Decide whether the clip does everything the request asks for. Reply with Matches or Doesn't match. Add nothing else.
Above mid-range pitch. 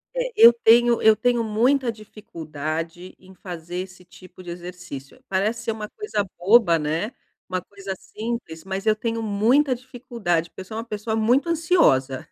Matches